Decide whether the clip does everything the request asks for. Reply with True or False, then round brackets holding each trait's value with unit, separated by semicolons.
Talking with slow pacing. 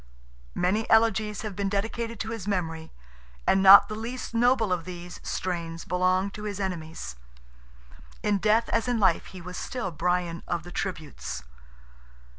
False (155 wpm)